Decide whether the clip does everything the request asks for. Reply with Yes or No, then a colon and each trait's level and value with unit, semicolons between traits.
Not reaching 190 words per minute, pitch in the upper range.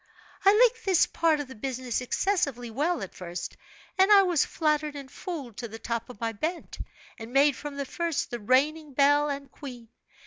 No: average, 195 wpm; very high, 280 Hz